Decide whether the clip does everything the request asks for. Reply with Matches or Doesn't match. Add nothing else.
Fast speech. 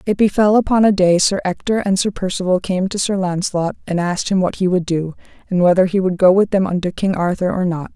Matches